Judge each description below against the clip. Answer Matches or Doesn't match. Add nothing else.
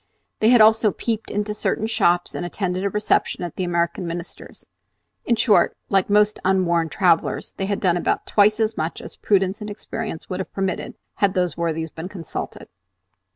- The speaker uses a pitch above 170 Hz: Matches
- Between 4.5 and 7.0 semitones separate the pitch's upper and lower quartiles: Doesn't match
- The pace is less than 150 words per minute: Doesn't match